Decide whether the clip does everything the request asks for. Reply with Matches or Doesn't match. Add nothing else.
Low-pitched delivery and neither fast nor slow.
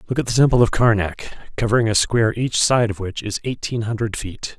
Doesn't match